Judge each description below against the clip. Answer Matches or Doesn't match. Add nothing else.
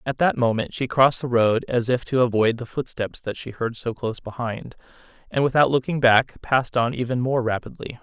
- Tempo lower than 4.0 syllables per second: Doesn't match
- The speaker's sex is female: Doesn't match